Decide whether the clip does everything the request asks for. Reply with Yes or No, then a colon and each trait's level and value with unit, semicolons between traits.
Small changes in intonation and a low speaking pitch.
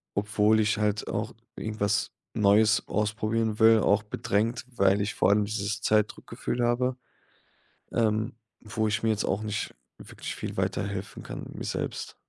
Yes: narrow, 1.2 semitones; low, 105 Hz